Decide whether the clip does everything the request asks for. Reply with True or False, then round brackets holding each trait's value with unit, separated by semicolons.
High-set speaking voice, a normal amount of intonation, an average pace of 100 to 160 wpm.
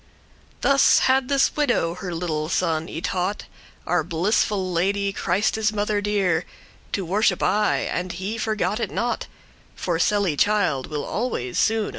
True (195 Hz; 3.7 semitones; 150 wpm)